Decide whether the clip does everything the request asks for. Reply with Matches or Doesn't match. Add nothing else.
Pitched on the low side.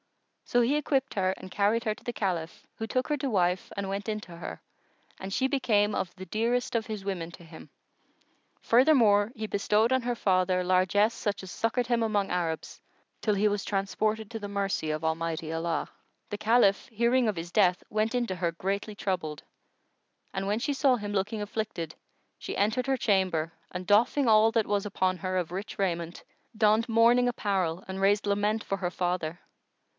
Doesn't match